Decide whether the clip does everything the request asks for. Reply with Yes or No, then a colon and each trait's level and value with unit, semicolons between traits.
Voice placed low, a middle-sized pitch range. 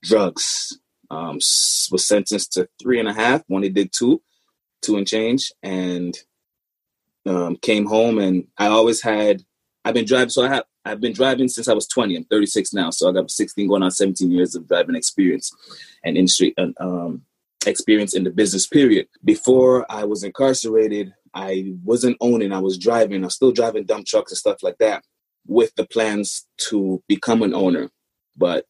Yes: low, 105 Hz; average, 4.2 semitones